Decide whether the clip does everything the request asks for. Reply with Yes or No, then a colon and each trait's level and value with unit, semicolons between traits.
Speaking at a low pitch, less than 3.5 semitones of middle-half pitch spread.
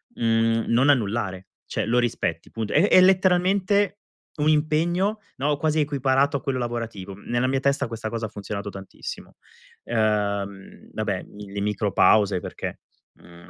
No: low, 120 Hz; wide, 6.2 semitones